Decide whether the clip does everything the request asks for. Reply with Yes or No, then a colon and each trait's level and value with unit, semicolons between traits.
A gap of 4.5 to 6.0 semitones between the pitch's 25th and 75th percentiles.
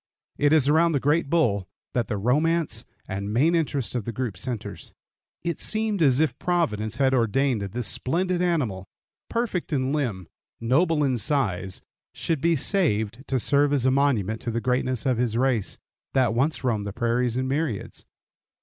Yes: average, 5.3 semitones